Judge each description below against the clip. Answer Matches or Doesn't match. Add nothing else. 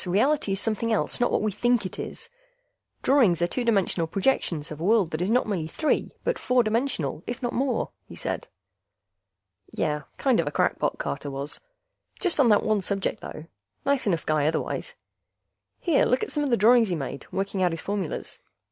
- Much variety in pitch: Matches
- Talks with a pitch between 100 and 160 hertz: Doesn't match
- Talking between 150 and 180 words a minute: Doesn't match